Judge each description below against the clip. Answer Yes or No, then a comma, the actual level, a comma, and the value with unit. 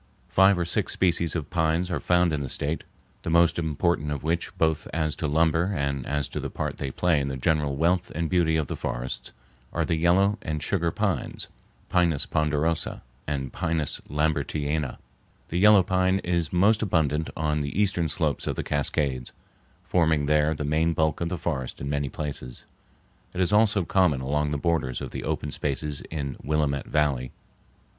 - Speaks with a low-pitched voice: Yes, very low, 80 Hz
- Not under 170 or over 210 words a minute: Yes, average, 180 wpm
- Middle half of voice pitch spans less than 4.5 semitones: Yes, average, 3.0 semitones